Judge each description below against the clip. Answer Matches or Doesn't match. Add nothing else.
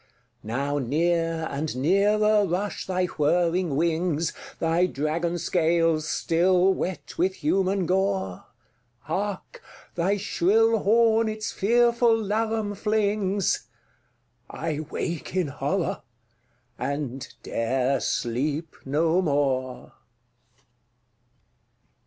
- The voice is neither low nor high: Matches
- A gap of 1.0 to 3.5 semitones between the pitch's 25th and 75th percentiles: Doesn't match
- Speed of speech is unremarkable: Doesn't match